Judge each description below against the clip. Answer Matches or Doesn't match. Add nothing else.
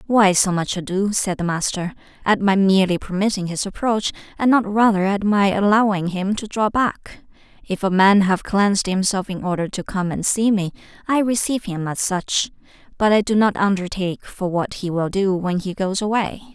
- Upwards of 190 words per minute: Matches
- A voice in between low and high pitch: Doesn't match